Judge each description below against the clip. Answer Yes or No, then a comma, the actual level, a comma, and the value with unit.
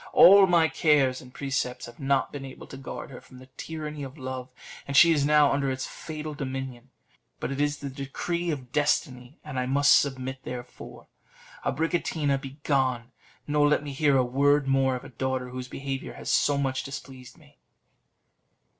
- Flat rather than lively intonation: Yes, narrow, 2.1 semitones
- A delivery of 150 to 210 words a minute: Yes, average, 180 wpm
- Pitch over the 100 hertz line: Yes, low, 135 Hz